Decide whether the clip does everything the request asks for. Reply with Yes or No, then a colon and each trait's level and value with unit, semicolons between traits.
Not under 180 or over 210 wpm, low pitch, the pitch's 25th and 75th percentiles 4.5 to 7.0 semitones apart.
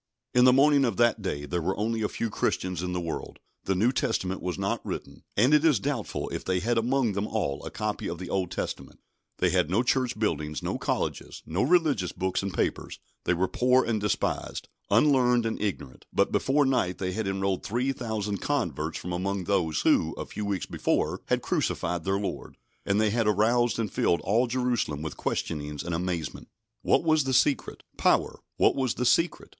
Yes: average, 200 wpm; low, 105 Hz; average, 5.1 semitones